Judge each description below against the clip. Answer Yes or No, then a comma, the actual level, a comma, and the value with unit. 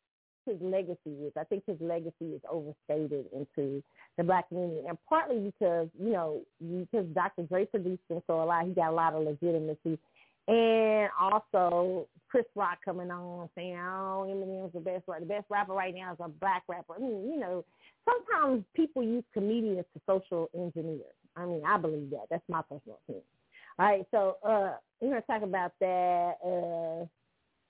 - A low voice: No, medium, 180 Hz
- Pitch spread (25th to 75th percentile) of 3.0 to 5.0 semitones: Yes, average, 3.7 semitones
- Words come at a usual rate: Yes, average, 180 wpm